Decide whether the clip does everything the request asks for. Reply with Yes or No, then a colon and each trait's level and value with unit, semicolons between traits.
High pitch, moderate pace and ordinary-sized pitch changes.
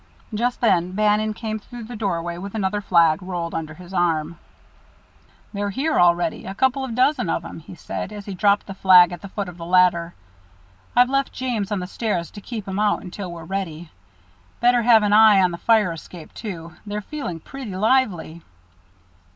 Yes: high, 195 Hz; average, 190 wpm; average, 3.9 semitones